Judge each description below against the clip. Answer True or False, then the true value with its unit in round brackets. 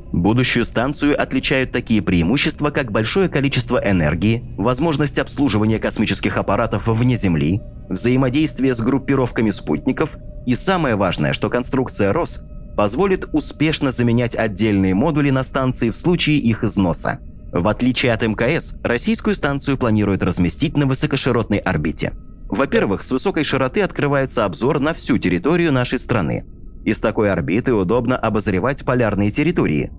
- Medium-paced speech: True (130 wpm)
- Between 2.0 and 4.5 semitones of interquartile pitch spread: False (4.9 semitones)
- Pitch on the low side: True (125 Hz)